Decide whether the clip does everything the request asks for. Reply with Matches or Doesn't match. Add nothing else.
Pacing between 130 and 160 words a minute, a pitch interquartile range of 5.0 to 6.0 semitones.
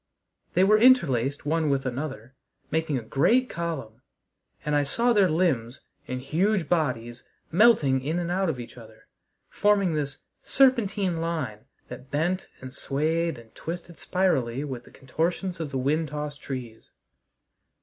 Matches